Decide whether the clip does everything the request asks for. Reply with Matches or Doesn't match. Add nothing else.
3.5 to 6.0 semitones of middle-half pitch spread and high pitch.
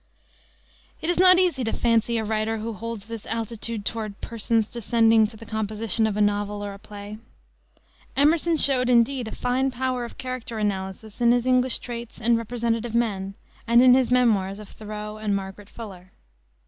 Doesn't match